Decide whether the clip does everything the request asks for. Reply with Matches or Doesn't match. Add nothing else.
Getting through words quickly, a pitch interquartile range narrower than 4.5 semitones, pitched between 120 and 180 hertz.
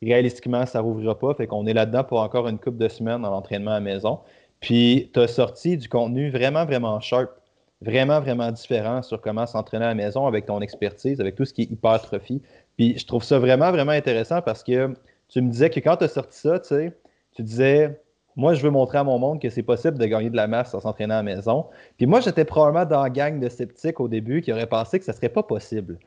Matches